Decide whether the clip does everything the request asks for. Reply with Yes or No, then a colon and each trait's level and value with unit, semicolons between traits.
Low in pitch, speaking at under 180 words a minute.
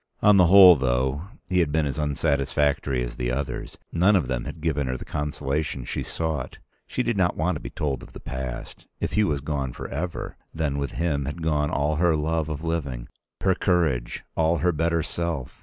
No: very low, 75 Hz; fast, 205 wpm